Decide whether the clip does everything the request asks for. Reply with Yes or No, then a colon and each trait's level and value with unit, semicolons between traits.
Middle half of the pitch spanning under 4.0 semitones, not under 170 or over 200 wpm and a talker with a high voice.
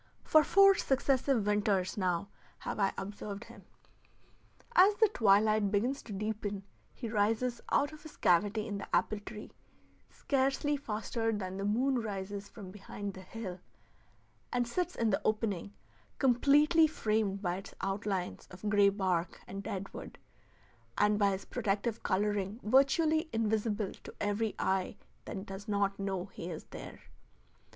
No: average, 3.4 semitones; average, 145 wpm; high, 210 Hz